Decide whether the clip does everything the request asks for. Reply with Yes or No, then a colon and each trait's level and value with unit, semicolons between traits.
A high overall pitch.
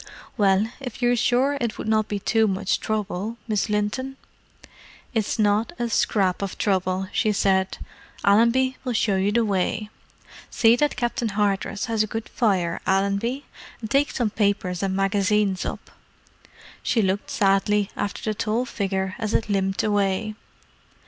Yes: high, 210 Hz